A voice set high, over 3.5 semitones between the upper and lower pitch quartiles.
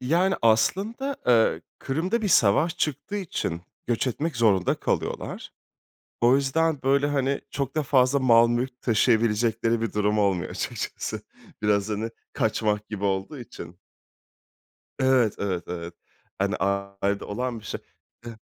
No: low, 115 Hz; average, 4.9 semitones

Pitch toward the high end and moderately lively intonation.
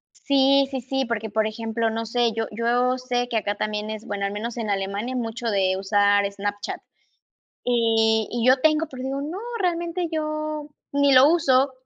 Yes: high, 235 Hz; average, 4.1 semitones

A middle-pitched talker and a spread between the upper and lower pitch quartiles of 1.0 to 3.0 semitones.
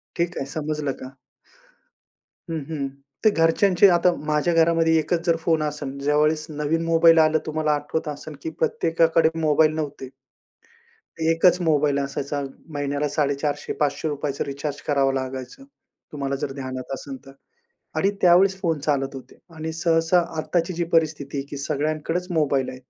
Yes: medium, 155 Hz; narrow, 2.5 semitones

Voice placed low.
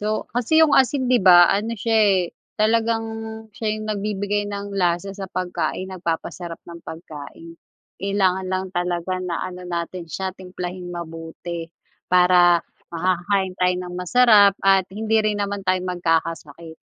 No: medium, 185 Hz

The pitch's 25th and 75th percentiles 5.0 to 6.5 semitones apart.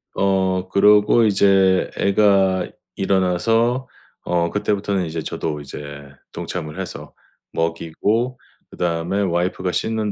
No: average, 3.1 semitones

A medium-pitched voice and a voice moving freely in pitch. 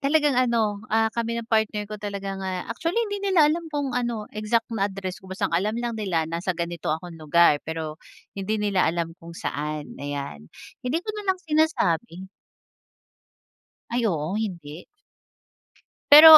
No: high, 205 Hz; wide, 6.1 semitones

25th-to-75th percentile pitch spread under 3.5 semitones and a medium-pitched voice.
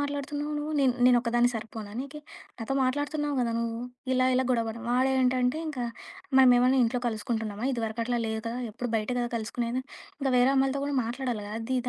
No: narrow, 2.5 semitones; very high, 250 Hz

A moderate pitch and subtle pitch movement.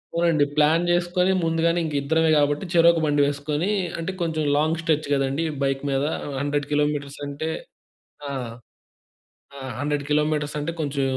Yes: medium, 150 Hz; narrow, 2.2 semitones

